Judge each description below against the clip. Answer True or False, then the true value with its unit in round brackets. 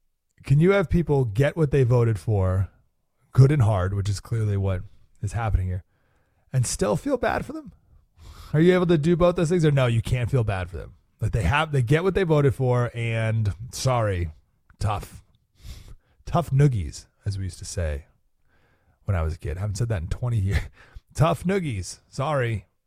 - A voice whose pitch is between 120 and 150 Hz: False (110 Hz)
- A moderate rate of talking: True (195 wpm)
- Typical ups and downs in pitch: False (6.3 semitones)